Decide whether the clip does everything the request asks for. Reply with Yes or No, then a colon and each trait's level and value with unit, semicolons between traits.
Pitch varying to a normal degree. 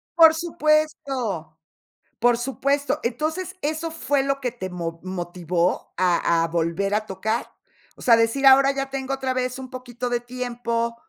No: wide, 5.9 semitones